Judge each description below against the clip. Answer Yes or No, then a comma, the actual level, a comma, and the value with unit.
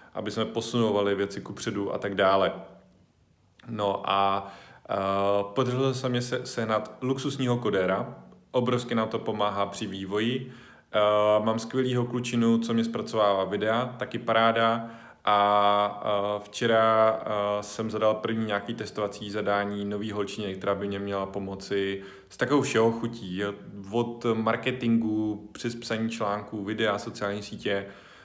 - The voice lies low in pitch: Yes, low, 110 Hz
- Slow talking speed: No, average, 135 wpm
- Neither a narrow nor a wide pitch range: No, narrow, 2.3 semitones